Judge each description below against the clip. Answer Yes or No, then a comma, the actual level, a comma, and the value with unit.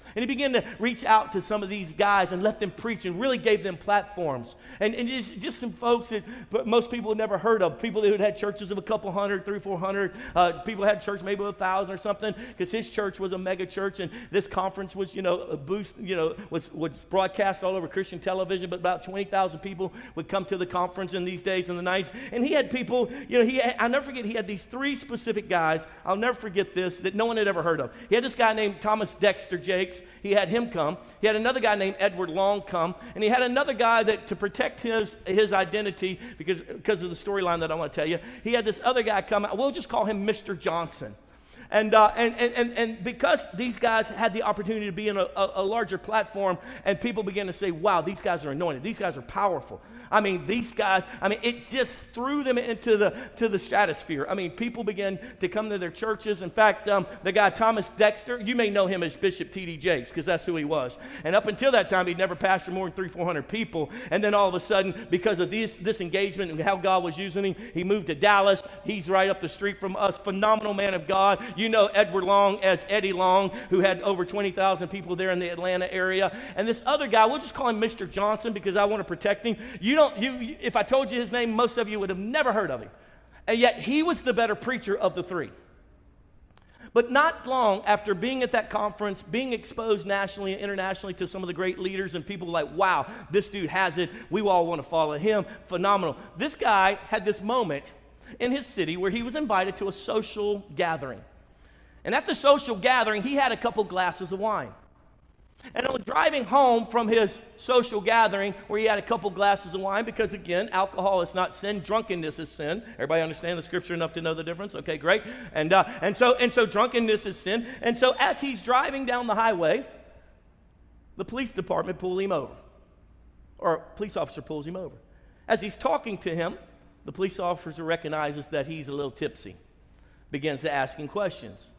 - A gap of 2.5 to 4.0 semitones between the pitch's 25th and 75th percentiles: Yes, average, 3.3 semitones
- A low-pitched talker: No, high, 200 Hz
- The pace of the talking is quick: Yes, fast, 230 wpm